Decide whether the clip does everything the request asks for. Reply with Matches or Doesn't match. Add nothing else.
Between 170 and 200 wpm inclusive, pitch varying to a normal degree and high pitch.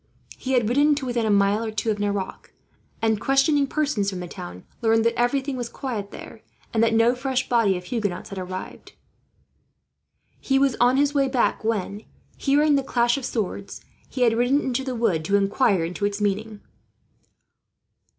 Matches